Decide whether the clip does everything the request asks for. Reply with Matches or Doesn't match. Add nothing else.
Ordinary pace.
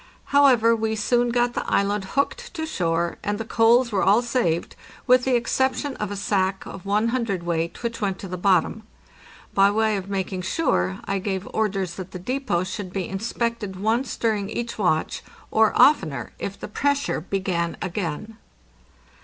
Matches